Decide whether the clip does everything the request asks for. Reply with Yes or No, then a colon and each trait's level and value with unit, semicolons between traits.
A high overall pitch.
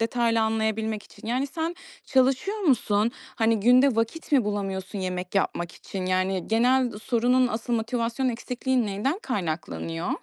Yes: high, 225 Hz